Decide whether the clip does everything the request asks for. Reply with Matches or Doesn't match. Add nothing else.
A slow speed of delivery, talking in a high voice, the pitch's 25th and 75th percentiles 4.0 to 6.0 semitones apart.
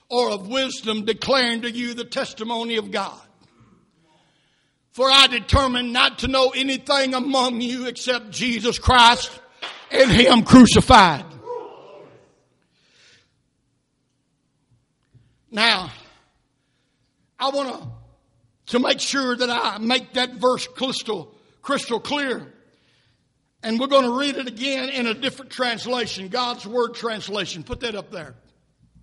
Matches